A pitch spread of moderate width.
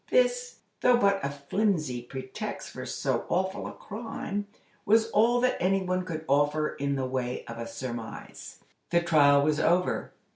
No: wide, 6.7 semitones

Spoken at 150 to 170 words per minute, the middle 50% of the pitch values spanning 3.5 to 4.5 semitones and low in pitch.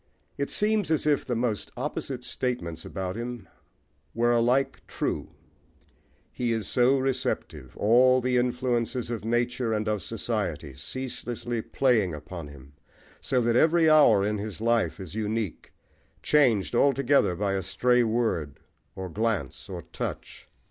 No: average, 140 wpm; average, 3.8 semitones; low, 115 Hz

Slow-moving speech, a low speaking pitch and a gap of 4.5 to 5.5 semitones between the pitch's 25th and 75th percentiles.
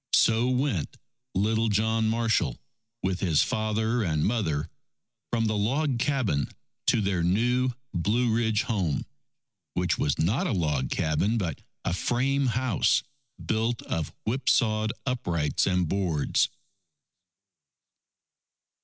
Yes: slow, 115 wpm; low, 110 Hz; average, 5.1 semitones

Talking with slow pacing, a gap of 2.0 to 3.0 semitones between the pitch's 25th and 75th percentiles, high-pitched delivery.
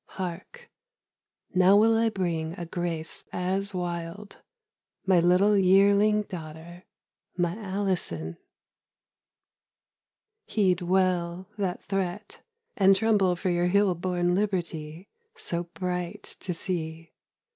No: slow, 105 wpm; narrow, 2.4 semitones; medium, 180 Hz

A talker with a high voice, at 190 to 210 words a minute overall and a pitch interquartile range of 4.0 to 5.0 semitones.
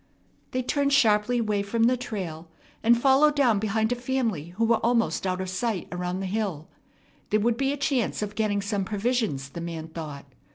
Yes: high, 215 Hz; average, 195 wpm; average, 4.6 semitones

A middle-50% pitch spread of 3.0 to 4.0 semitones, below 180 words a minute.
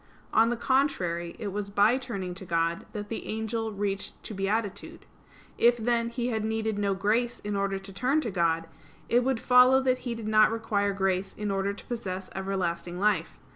No: average, 3.3 semitones; average, 190 wpm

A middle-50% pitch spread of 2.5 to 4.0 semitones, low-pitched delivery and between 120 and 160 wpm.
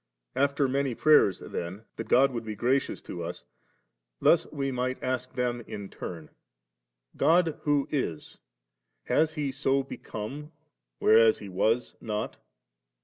No: average, 4.7 semitones; low, 125 Hz; average, 140 wpm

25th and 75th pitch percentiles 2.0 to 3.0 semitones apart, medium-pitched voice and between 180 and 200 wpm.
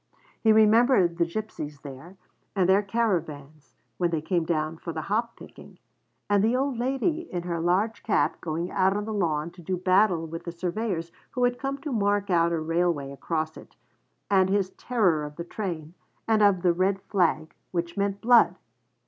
No: average, 4.3 semitones; medium, 180 Hz; average, 185 wpm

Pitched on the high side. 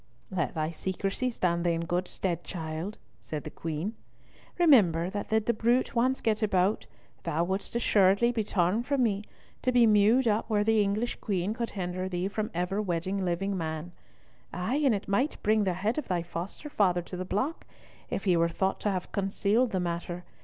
Yes: high, 195 Hz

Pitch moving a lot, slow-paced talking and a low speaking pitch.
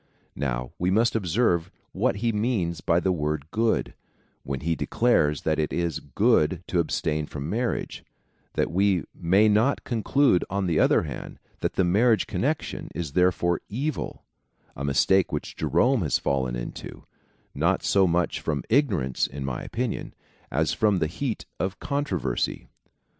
No: wide, 6.2 semitones; average, 160 wpm; very low, 90 Hz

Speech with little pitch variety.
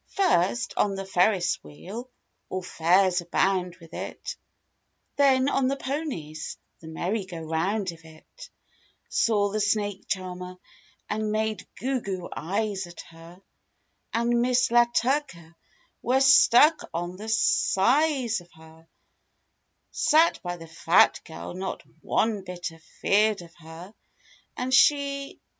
No: wide, 5.5 semitones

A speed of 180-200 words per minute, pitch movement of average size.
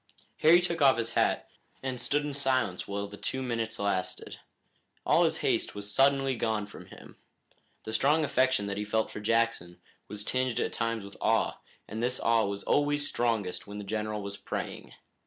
Yes: average, 185 wpm; average, 4.3 semitones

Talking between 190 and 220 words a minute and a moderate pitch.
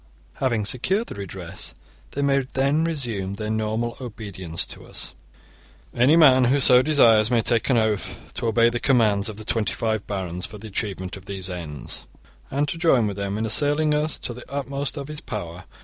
No: average, 195 wpm; low, 115 Hz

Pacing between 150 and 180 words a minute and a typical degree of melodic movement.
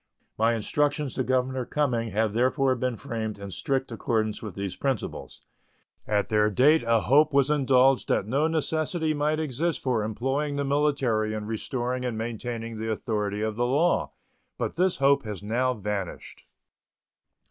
Yes: average, 160 wpm; average, 4.4 semitones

